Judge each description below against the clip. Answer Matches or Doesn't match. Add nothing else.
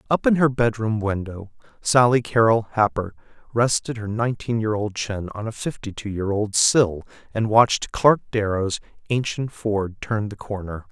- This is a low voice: Matches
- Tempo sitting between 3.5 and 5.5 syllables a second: Matches